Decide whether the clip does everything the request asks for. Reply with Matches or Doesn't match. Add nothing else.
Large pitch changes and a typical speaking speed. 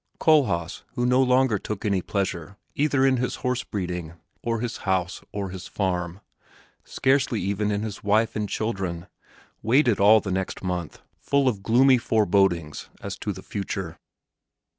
Doesn't match